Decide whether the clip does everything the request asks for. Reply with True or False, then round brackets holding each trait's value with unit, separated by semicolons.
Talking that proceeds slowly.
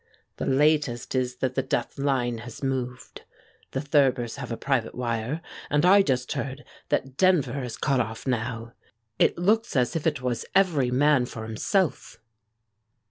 False (160 wpm)